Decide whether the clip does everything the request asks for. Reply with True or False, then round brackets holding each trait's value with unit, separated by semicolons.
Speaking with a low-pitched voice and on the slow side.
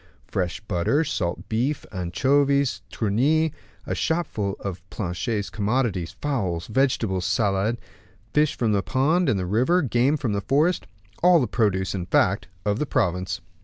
False (110 Hz; 145 wpm)